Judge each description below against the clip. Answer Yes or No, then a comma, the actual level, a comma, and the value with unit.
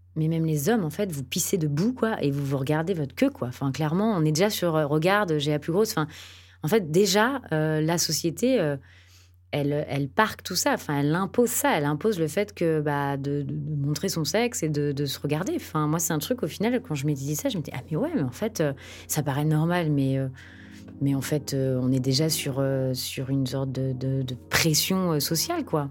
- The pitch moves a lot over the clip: No, average, 4.2 semitones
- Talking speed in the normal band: No, fast, 250 wpm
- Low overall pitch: No, medium, 150 Hz